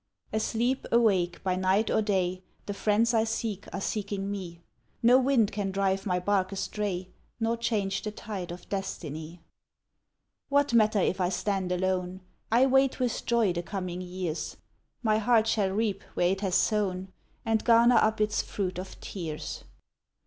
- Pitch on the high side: Yes, high, 200 Hz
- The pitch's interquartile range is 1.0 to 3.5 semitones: Yes, average, 3.2 semitones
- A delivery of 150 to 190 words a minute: Yes, average, 160 wpm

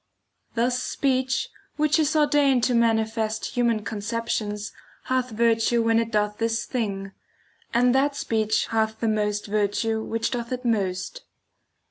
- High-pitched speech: Yes, high, 230 Hz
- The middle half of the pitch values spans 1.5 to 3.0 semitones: Yes, narrow, 2.5 semitones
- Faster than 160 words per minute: No, slow, 135 wpm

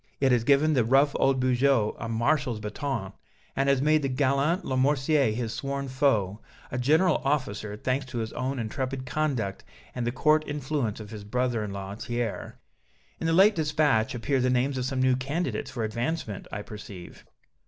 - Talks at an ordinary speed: Yes, average, 180 wpm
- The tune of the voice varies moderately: Yes, average, 3.8 semitones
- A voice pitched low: Yes, low, 130 Hz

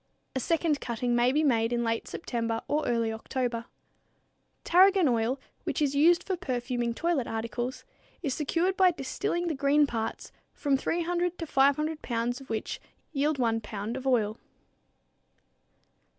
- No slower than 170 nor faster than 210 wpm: No, average, 150 wpm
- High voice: Yes, very high, 265 Hz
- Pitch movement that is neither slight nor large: Yes, average, 5.0 semitones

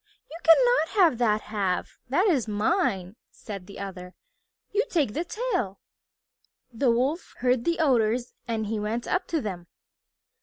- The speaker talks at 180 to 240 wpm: No, average, 150 wpm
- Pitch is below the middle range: No, high, 235 Hz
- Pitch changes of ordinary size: No, wide, 8.0 semitones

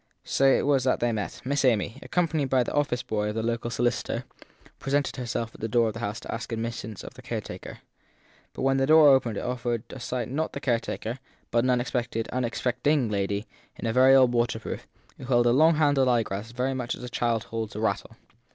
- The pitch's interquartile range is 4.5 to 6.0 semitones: No, average, 2.7 semitones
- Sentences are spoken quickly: Yes, fast, 220 wpm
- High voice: No, low, 120 Hz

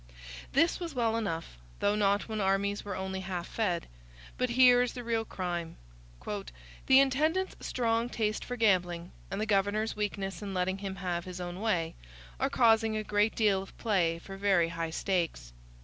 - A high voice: Yes, high, 200 Hz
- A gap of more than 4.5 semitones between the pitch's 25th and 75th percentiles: No, average, 3.6 semitones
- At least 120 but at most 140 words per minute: No, average, 175 wpm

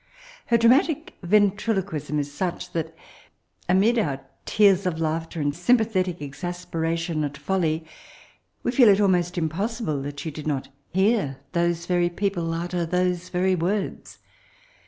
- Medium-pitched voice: Yes, medium, 175 Hz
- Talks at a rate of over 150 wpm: No, average, 140 wpm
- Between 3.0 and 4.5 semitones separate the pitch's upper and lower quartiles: Yes, average, 3.6 semitones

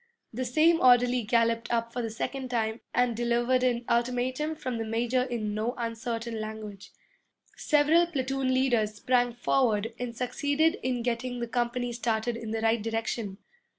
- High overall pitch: Yes, high, 240 Hz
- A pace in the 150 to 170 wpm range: Yes, average, 155 wpm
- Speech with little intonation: Yes, narrow, 2.0 semitones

